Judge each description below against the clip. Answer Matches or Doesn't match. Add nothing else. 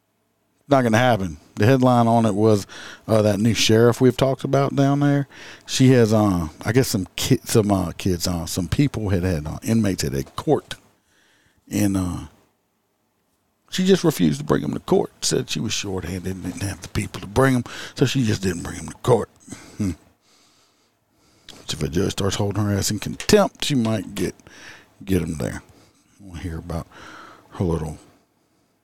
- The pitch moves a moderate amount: Matches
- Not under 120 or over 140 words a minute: Doesn't match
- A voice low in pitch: Matches